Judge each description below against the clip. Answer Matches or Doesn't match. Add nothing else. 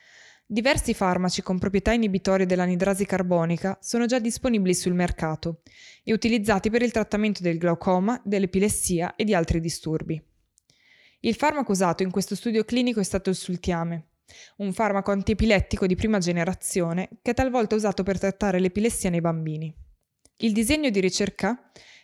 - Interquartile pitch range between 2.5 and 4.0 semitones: Matches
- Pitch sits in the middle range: Doesn't match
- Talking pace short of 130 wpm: Doesn't match